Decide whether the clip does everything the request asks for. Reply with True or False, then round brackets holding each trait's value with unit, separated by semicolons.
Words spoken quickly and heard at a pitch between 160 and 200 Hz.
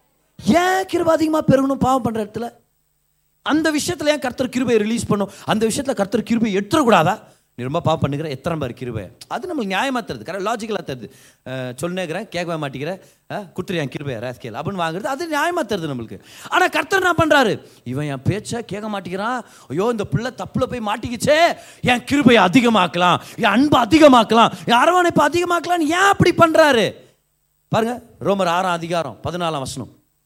False (155 wpm; 210 Hz)